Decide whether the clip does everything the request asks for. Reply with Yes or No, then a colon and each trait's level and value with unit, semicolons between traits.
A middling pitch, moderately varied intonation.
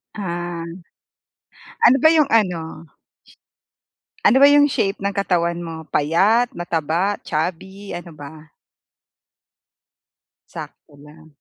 Yes: medium, 175 Hz; average, 4.0 semitones